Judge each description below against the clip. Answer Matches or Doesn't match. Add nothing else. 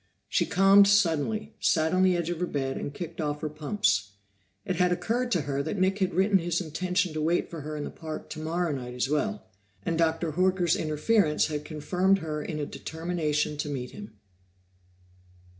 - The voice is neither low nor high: Matches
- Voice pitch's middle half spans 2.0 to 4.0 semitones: Matches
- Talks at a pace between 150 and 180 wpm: Doesn't match